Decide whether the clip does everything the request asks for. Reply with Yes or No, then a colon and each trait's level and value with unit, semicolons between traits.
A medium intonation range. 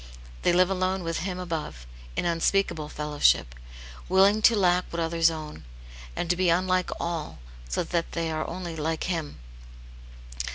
No: narrow, 2.2 semitones